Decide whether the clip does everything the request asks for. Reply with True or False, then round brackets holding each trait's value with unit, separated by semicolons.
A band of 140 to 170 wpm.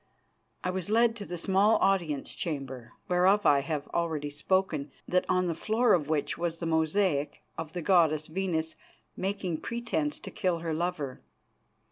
True (160 wpm)